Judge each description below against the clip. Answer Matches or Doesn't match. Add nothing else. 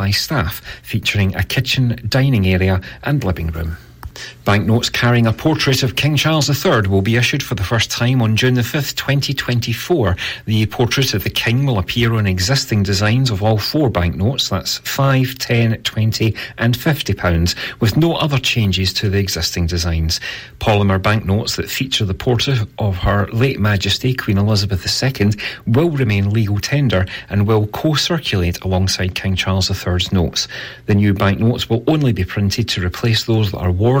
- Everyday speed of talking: Matches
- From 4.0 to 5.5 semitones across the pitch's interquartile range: Matches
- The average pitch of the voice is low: Matches